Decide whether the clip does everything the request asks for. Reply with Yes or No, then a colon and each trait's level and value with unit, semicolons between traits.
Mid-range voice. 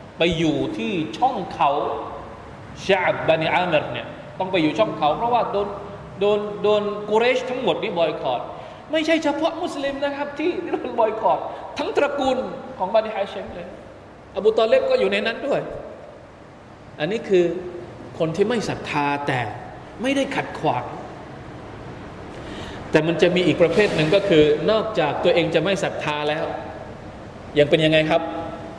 Yes: medium, 180 Hz